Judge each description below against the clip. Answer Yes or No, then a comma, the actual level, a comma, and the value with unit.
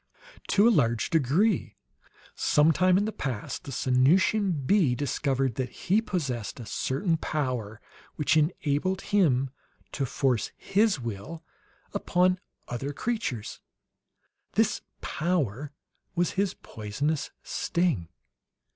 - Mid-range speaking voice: Yes, medium, 150 Hz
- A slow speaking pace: Yes, slow, 110 wpm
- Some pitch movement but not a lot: No, wide, 6.3 semitones